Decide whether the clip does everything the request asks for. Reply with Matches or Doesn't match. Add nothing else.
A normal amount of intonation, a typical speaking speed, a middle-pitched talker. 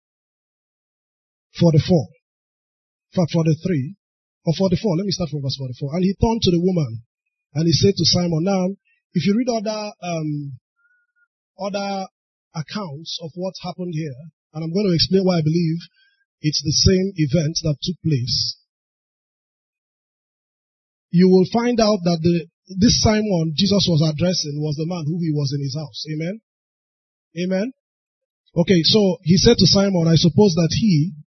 Matches